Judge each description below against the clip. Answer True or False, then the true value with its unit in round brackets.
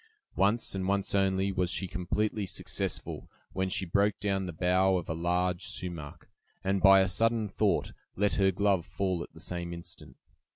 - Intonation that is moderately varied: False (1.8 semitones)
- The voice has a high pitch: False (95 Hz)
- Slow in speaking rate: False (175 wpm)